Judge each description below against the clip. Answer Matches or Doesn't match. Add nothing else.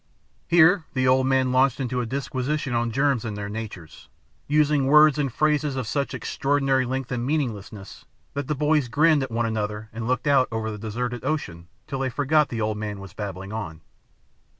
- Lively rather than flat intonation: Doesn't match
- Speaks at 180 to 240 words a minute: Matches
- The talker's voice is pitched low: Matches